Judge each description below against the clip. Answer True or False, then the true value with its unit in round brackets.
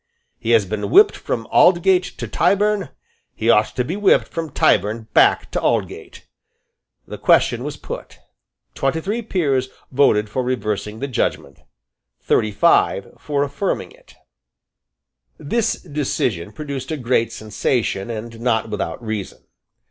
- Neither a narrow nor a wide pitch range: False (6.6 semitones)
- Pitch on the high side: False (125 Hz)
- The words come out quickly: False (135 wpm)